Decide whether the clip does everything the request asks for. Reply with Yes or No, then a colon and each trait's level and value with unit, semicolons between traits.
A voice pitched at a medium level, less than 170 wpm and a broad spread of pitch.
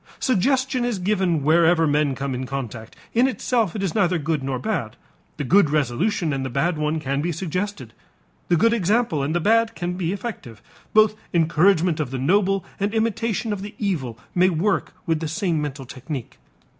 No: medium, 170 Hz; average, 185 wpm; wide, 5.9 semitones